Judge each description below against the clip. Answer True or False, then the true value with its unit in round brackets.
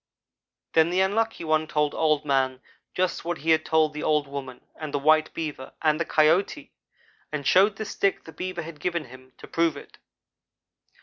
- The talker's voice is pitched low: False (155 Hz)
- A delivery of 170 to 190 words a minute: True (185 wpm)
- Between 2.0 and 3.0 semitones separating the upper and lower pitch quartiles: True (2.7 semitones)